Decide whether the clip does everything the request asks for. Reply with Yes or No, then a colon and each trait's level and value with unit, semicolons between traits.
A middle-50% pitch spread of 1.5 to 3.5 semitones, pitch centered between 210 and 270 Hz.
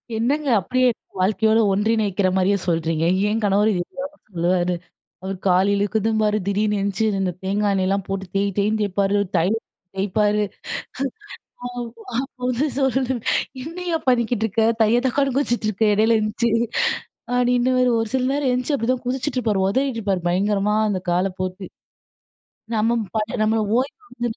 No: average, 4.0 semitones; high, 215 Hz